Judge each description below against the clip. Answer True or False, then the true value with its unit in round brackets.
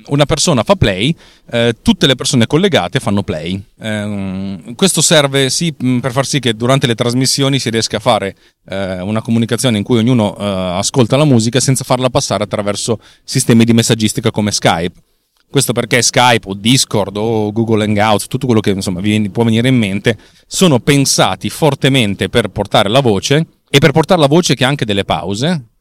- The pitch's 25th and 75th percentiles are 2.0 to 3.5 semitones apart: False (4.6 semitones)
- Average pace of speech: False (185 wpm)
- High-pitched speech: False (120 Hz)